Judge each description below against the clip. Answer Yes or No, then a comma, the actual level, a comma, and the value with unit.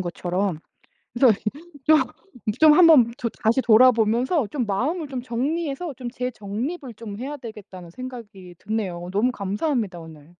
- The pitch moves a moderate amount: Yes, average, 4.9 semitones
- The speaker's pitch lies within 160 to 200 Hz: No, high, 235 Hz